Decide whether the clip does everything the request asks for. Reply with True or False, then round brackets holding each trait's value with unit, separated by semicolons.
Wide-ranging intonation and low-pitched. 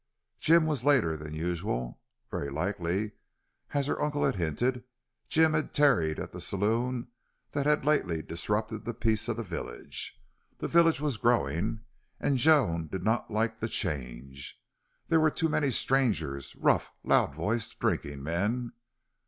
True (8.6 semitones; 110 Hz)